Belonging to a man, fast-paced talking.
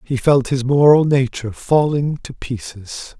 No: male; average, 150 wpm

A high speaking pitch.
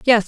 Yes: high, 230 Hz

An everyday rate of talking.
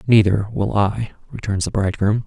Yes: average, 160 wpm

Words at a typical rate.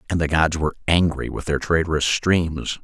Yes: average, 190 wpm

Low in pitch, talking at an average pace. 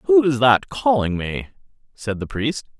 Yes: low, 120 Hz; average, 170 wpm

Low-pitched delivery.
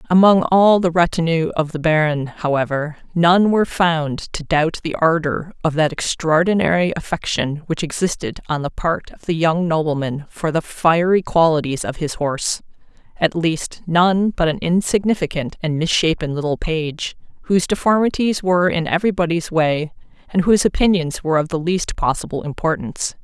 No: medium, 165 Hz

